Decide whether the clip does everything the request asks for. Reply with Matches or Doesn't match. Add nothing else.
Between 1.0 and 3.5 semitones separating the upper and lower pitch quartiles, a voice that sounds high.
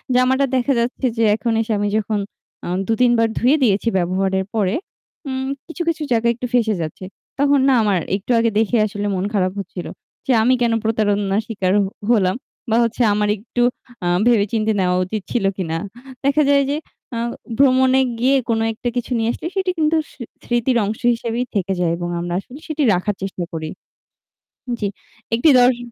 Doesn't match